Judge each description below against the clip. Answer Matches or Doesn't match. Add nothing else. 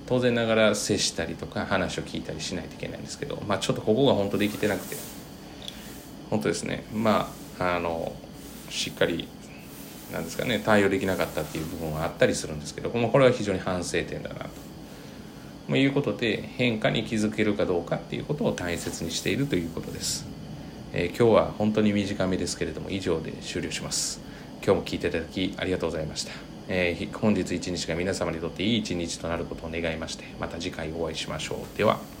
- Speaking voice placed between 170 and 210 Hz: Doesn't match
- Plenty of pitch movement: Doesn't match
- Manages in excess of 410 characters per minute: Matches